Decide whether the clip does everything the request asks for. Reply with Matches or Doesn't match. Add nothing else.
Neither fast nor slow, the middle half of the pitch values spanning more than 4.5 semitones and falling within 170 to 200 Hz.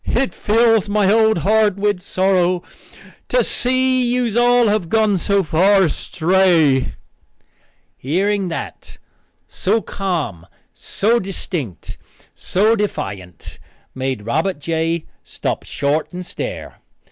Doesn't match